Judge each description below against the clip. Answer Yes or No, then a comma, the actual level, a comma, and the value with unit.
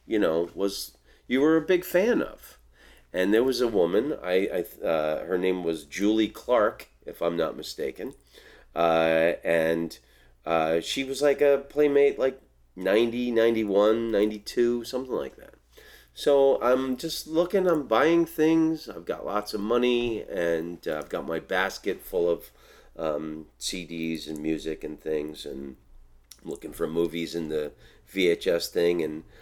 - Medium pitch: No, low, 105 Hz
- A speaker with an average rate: Yes, average, 155 wpm